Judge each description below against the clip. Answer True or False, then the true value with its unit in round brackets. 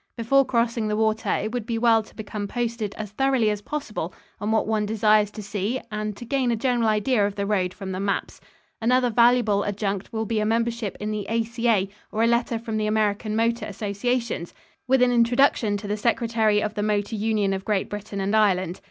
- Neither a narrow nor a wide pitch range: False (2.1 semitones)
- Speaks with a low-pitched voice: False (215 Hz)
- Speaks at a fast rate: True (210 wpm)